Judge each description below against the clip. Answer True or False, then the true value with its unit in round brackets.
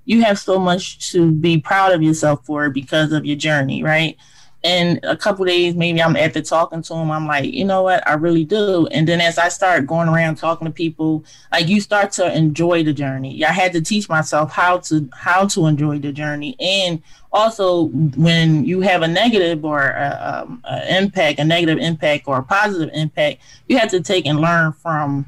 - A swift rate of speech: True (210 wpm)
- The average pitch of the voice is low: False (165 Hz)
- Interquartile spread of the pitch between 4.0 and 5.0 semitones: False (3.1 semitones)